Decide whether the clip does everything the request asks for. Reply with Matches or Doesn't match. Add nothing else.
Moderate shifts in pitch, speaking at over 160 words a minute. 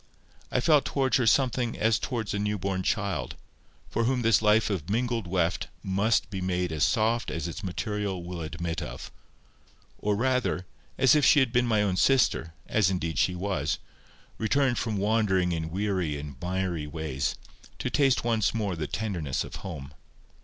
Matches